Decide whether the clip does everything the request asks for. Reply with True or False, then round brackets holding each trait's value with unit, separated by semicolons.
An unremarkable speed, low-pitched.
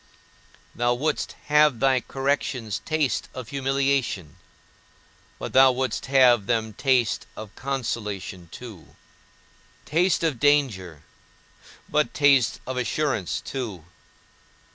False (100 wpm; 130 Hz)